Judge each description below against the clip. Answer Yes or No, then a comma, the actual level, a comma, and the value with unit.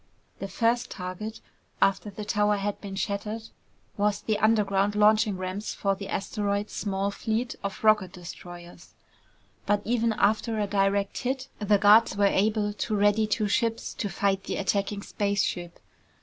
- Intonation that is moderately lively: No, narrow, 1.5 semitones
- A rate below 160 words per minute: Yes, average, 150 wpm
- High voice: Yes, high, 205 Hz